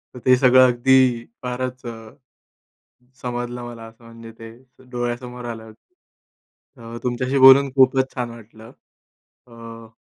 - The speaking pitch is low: Yes, low, 120 Hz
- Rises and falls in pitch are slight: Yes, narrow, 1.8 semitones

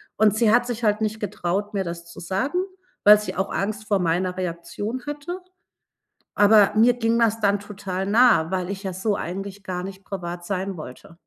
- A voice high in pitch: Yes, high, 200 Hz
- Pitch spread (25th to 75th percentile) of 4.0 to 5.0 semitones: No, average, 2.9 semitones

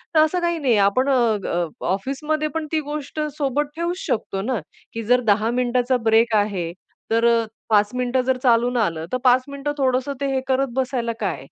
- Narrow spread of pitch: No, average, 3.6 semitones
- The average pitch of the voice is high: Yes, very high, 250 Hz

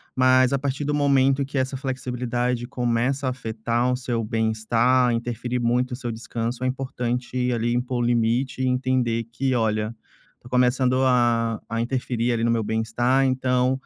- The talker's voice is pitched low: Yes, low, 125 Hz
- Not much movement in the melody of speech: Yes, narrow, 1.8 semitones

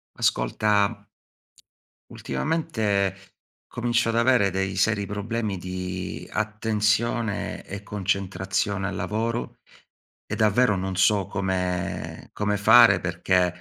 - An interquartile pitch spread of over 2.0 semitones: Yes, narrow, 2.6 semitones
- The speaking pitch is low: Yes, low, 100 Hz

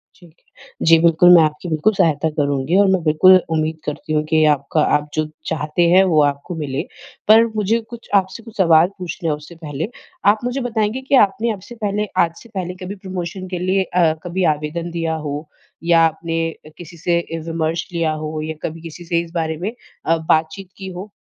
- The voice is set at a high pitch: No, medium, 170 Hz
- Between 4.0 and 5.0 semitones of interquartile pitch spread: No, average, 3.2 semitones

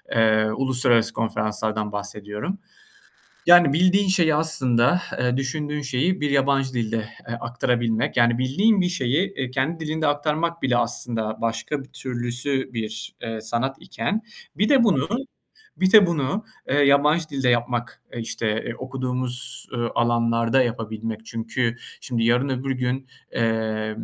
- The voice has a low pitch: Yes, low, 125 Hz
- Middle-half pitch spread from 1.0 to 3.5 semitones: No, average, 4.1 semitones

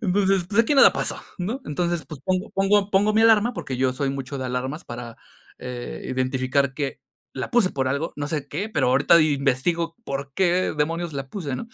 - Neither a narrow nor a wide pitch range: No, wide, 6.3 semitones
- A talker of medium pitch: Yes, medium, 150 Hz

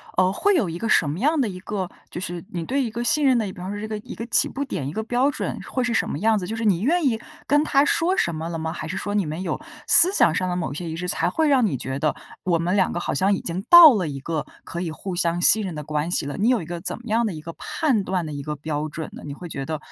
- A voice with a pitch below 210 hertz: Yes, medium, 185 Hz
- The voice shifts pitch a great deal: Yes, wide, 6.2 semitones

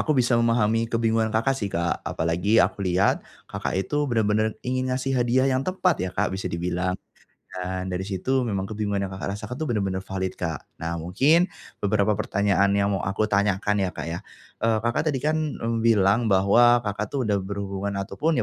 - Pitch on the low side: Yes, low, 105 Hz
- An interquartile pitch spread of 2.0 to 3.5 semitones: No, average, 3.9 semitones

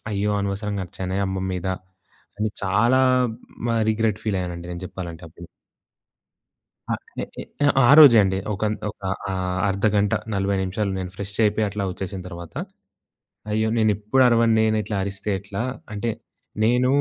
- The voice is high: No, low, 100 Hz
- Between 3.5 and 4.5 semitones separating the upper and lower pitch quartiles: No, narrow, 2.4 semitones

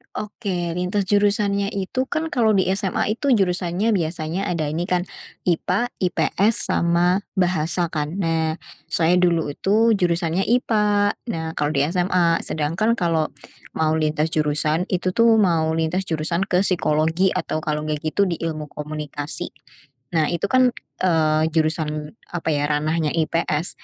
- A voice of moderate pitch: Yes, medium, 170 Hz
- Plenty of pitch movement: No, average, 3.8 semitones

